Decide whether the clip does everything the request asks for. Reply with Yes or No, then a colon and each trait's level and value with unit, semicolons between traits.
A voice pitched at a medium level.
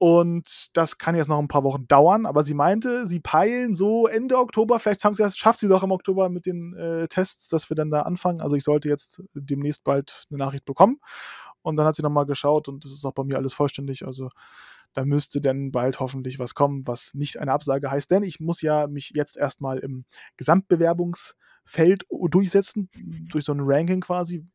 Yes: medium, 155 Hz